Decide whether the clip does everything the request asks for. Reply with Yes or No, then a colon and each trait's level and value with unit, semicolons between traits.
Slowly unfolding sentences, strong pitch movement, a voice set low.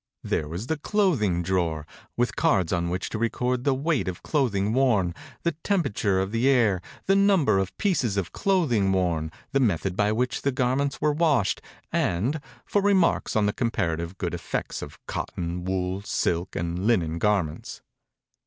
No: average, 175 wpm; wide, 7.3 semitones; low, 105 Hz